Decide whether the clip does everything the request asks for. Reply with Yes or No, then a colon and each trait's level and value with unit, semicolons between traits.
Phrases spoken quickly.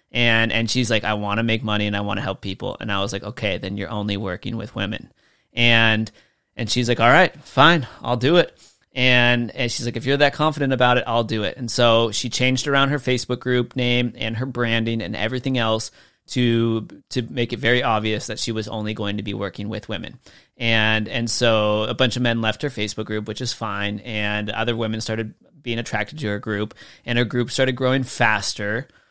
Yes: fast, 225 wpm